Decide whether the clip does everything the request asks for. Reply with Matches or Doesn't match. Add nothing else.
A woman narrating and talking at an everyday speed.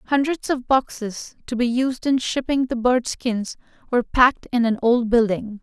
Matches